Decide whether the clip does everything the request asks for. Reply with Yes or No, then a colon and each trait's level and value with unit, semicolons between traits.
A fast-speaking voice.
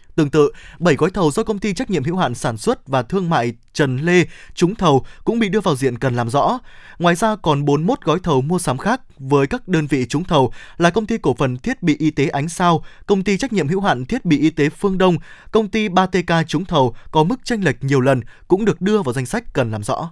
Yes: fast, 260 wpm